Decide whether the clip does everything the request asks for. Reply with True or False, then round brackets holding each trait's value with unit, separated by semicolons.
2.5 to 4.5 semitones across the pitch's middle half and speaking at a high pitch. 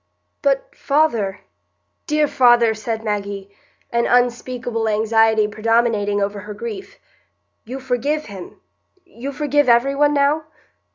False (4.9 semitones; 235 Hz)